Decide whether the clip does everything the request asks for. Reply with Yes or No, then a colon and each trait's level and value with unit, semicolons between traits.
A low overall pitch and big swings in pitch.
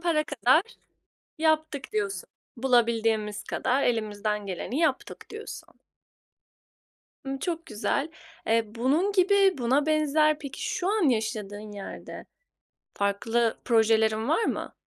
No: very high, 250 Hz; wide, 6.0 semitones